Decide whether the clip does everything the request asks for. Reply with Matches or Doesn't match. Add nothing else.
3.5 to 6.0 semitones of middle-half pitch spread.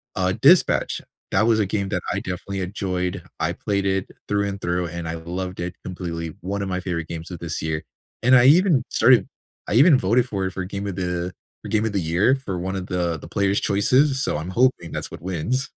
Doesn't match